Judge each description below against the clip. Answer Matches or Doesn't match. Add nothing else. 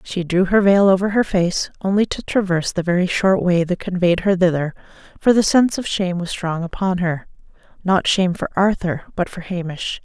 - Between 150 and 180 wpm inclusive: Doesn't match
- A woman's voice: Matches